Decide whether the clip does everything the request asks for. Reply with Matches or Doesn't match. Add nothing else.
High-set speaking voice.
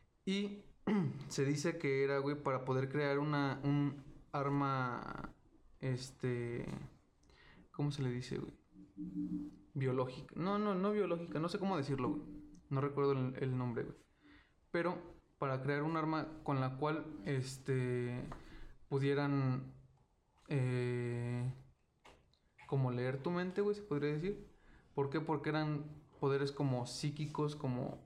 Doesn't match